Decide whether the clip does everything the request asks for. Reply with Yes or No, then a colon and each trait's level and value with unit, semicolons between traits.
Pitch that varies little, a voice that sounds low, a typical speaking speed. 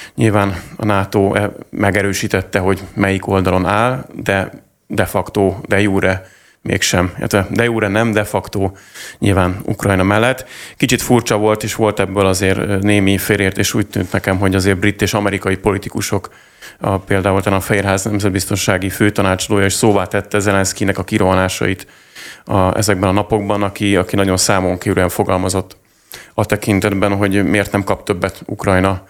Yes: narrow, 1.5 semitones; low, 100 Hz; average, 145 wpm